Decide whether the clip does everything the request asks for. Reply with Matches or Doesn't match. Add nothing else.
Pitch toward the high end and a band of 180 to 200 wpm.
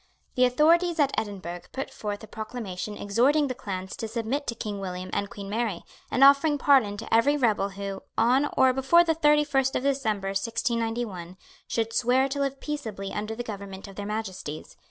Matches